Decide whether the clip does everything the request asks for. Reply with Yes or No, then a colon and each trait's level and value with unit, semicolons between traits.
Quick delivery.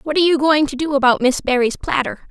Yes: fast, 260 wpm